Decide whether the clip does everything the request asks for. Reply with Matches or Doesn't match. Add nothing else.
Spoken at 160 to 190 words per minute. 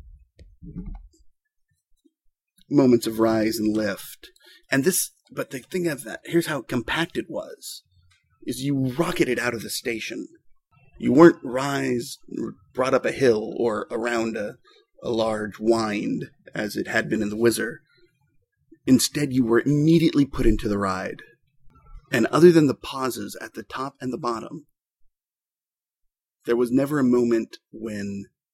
Doesn't match